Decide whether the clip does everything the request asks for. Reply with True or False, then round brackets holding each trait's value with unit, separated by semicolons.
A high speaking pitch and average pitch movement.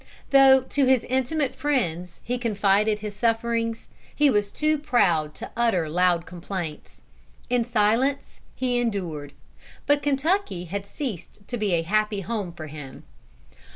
False (215 Hz; 6.3 semitones)